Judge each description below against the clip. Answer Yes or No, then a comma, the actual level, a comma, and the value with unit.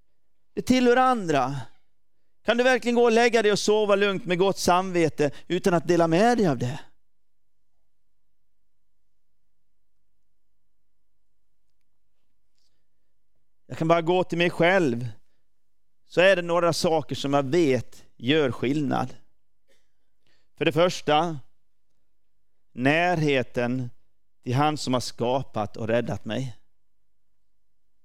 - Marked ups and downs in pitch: Yes, wide, 6.3 semitones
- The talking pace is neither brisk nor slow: No, slow, 110 wpm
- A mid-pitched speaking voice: Yes, medium, 160 Hz